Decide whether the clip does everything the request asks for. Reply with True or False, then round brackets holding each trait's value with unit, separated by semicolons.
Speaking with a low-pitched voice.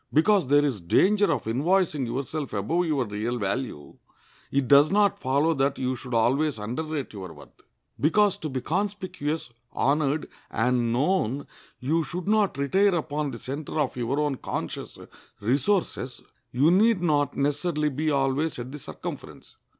False (145 Hz)